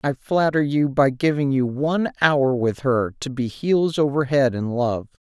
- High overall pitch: No, medium, 140 Hz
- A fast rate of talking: No, average, 195 wpm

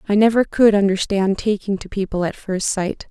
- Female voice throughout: Yes, female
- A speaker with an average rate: Yes, average, 195 wpm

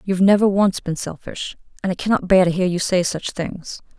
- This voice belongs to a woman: Yes, female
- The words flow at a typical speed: No, fast, 225 wpm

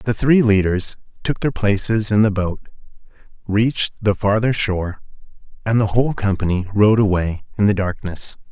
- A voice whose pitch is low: Yes, low, 105 Hz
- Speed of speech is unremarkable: Yes, average, 155 wpm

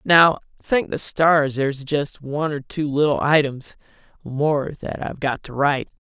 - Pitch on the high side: No, medium, 145 Hz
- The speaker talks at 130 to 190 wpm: Yes, average, 170 wpm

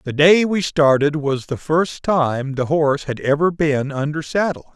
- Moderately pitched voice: Yes, medium, 150 Hz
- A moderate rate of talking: Yes, average, 190 wpm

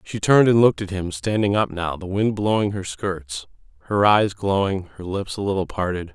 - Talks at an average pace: No, fast, 215 wpm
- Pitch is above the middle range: No, very low, 95 Hz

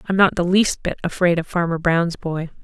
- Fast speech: Yes, fast, 230 wpm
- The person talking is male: No, female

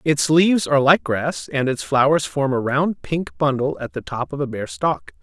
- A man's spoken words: Yes, male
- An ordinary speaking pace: No, fast, 230 wpm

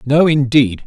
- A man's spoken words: Yes, male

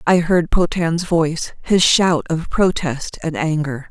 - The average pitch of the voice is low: No, medium, 165 Hz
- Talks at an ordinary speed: Yes, average, 155 wpm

